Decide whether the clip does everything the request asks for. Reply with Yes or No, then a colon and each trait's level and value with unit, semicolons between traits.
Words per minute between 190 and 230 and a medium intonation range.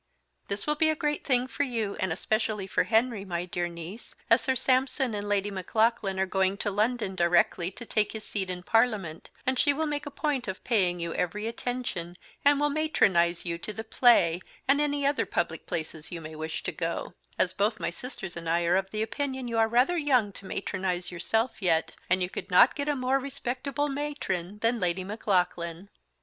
No: fast, 205 wpm; wide, 6.0 semitones